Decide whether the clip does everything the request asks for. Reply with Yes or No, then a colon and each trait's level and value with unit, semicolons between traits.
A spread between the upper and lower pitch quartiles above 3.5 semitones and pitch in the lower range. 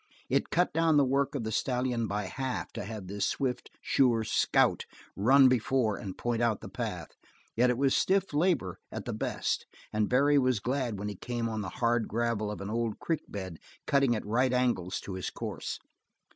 Yes: average, 4.1 semitones; low, 120 Hz